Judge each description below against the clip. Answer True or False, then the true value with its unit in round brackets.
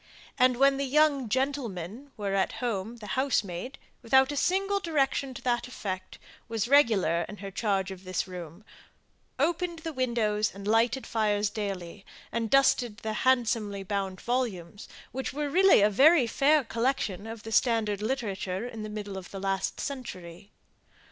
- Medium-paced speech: True (160 wpm)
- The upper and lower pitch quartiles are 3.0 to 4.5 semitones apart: False (5.1 semitones)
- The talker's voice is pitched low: False (225 Hz)